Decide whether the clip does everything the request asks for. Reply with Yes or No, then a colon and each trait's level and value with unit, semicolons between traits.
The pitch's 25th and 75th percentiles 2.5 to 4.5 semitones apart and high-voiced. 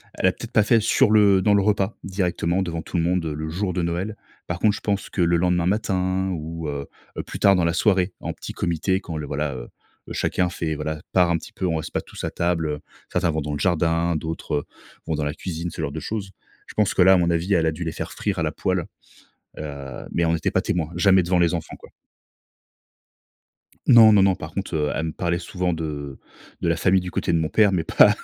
No: average, 2.9 semitones; very low, 85 Hz